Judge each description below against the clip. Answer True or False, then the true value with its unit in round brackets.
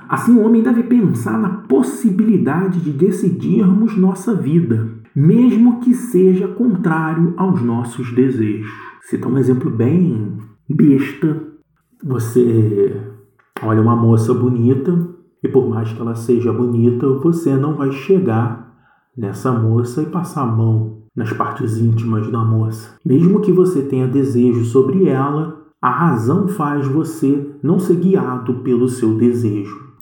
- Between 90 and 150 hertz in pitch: True (135 Hz)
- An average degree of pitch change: False (7.2 semitones)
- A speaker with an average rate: True (135 wpm)